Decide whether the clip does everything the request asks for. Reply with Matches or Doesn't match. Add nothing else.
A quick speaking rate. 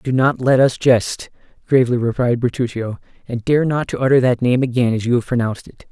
Matches